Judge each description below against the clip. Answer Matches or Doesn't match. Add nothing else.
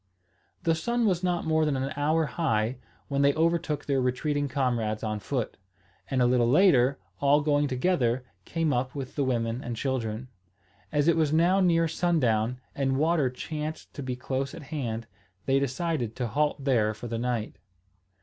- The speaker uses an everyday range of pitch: Matches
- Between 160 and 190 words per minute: Matches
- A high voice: Doesn't match